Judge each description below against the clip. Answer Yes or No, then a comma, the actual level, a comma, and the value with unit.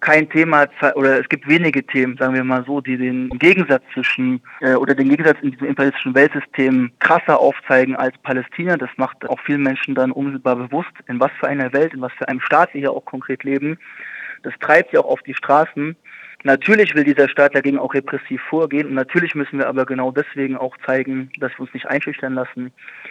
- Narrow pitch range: Yes, narrow, 2.1 semitones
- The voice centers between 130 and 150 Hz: Yes, low, 135 Hz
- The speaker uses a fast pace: Yes, fast, 210 wpm